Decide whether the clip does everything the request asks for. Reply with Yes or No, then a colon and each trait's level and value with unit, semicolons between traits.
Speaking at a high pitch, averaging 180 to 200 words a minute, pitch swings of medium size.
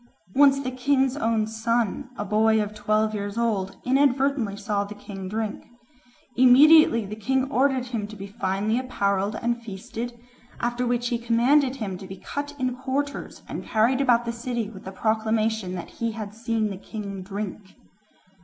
No: high, 225 Hz; average, 170 wpm; average, 3.5 semitones